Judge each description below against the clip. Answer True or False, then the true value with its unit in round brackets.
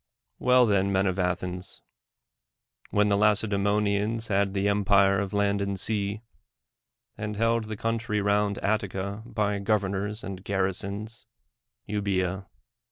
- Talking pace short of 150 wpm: True (135 wpm)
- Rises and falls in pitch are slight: True (1.3 semitones)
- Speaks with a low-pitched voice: True (100 Hz)